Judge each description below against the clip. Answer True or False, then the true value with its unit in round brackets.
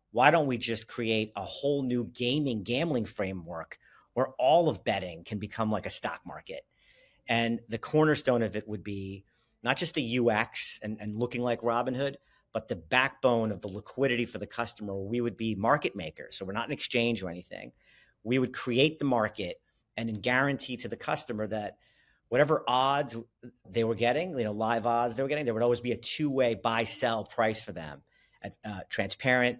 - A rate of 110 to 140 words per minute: False (195 wpm)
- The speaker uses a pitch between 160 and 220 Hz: False (120 Hz)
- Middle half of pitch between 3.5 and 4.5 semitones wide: False (2.7 semitones)